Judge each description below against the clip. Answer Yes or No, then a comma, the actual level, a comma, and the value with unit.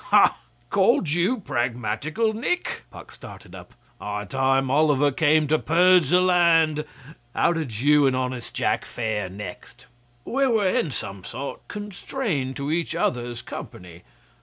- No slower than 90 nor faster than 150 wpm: Yes, average, 140 wpm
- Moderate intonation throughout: No, wide, 6.3 semitones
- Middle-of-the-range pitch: Yes, medium, 145 Hz